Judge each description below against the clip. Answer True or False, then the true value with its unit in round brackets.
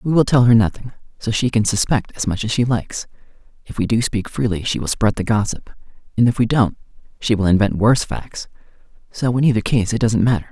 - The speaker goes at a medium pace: False (230 wpm)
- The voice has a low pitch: True (110 Hz)